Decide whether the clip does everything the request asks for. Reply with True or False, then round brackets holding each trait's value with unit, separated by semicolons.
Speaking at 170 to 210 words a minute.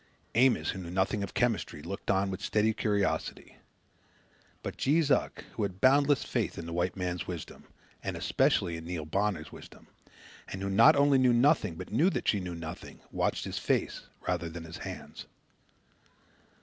True (175 wpm)